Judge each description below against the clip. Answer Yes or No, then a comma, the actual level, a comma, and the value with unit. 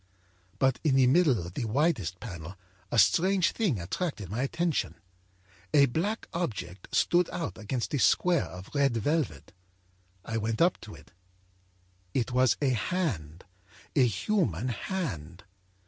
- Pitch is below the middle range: Yes, low, 125 Hz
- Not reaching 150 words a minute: Yes, average, 140 wpm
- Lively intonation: Yes, wide, 8.7 semitones